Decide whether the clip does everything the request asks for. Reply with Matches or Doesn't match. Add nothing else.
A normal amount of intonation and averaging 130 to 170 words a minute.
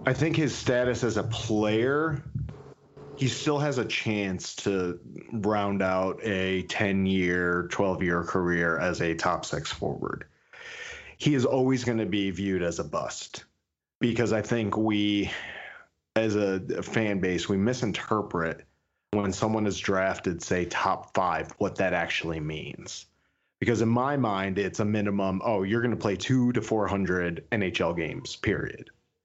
Matches